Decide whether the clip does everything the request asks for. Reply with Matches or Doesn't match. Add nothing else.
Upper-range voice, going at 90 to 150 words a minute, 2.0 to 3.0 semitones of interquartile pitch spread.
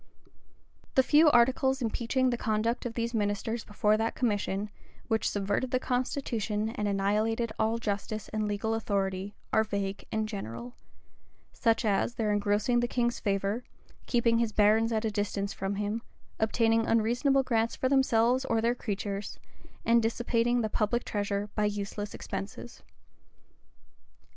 Matches